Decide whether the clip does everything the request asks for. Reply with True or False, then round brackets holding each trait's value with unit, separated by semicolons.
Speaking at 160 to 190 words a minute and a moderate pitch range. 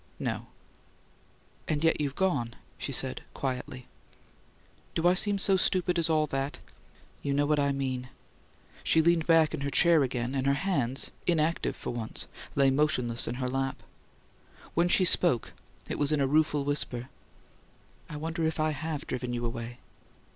True (165 wpm; 3.8 semitones)